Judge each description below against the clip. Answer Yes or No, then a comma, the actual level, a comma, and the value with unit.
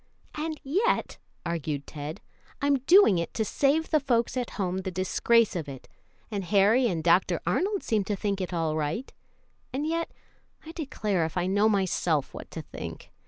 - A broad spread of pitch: Yes, wide, 8.0 semitones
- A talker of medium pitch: No, high, 200 Hz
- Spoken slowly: No, average, 175 wpm